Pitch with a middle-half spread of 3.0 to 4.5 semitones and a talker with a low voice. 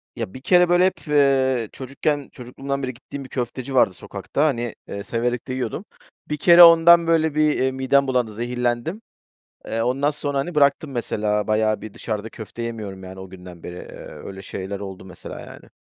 No: average, 5.0 semitones; low, 130 Hz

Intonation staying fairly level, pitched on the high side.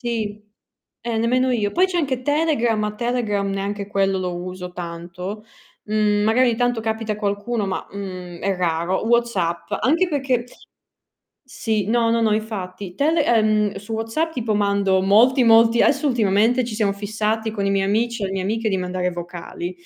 No: average, 3.4 semitones; high, 215 Hz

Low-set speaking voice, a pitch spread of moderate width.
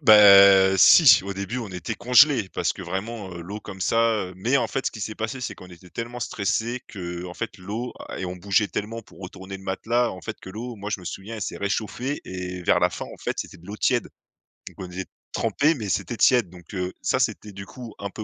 Yes: low, 100 Hz; average, 3.7 semitones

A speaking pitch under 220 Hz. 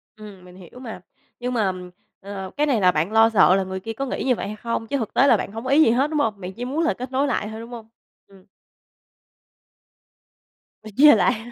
No: high, 225 Hz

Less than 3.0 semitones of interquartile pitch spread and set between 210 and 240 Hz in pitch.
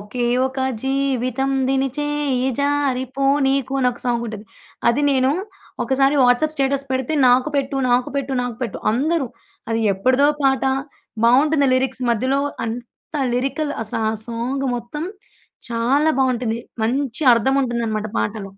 No: narrow, 2.5 semitones; very high, 260 Hz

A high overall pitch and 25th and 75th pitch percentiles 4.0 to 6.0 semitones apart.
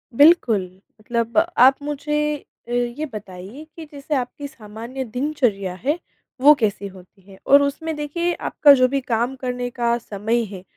Yes: very high, 250 Hz; average, 4.8 semitones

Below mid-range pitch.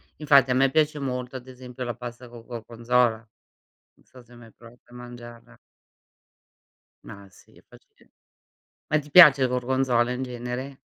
Yes: low, 125 Hz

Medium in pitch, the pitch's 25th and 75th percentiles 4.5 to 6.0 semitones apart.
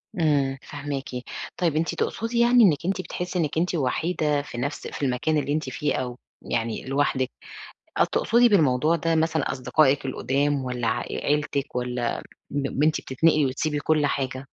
No: medium, 145 Hz; average, 3.4 semitones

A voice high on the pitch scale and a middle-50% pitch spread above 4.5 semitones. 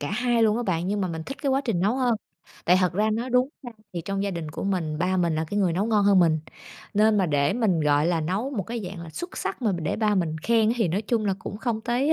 Yes: high, 200 Hz; average, 5.1 semitones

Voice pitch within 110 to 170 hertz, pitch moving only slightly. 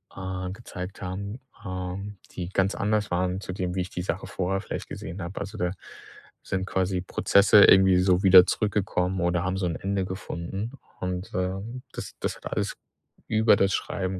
No: very low, 95 Hz; narrow, 1.5 semitones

